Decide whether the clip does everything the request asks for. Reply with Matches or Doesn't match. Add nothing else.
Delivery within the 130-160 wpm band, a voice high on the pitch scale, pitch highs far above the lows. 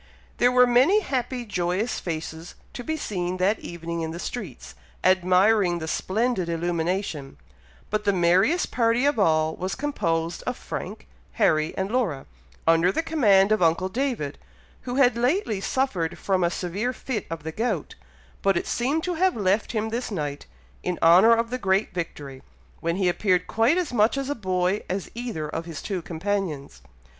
Doesn't match